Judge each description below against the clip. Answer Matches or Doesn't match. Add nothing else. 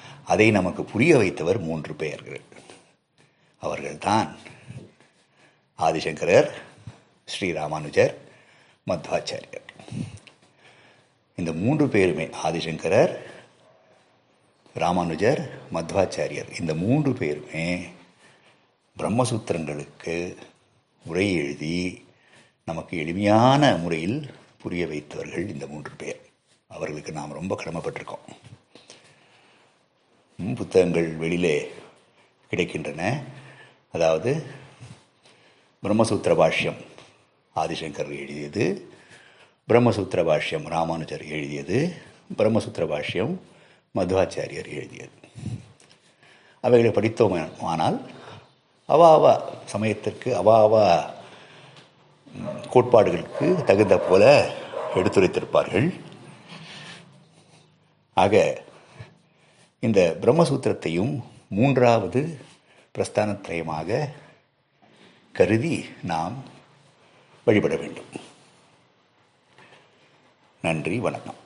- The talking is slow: Matches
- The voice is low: Matches